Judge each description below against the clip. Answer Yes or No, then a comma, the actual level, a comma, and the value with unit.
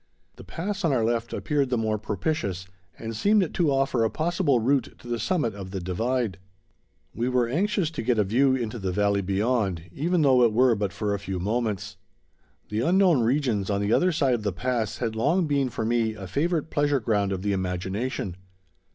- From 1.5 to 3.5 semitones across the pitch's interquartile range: No, wide, 5.5 semitones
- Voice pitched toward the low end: Yes, low, 115 Hz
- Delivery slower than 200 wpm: No, fast, 205 wpm